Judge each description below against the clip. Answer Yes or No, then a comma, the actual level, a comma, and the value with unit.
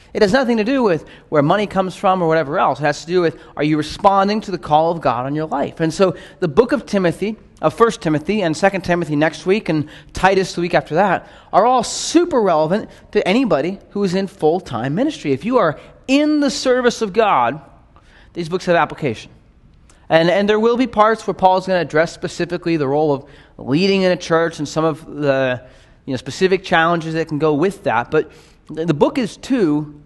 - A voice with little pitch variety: No, average, 4.6 semitones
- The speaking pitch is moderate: Yes, medium, 175 Hz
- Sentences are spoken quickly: Yes, fast, 220 wpm